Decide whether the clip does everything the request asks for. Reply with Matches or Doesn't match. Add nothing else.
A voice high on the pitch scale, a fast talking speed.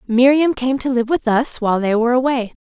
Matches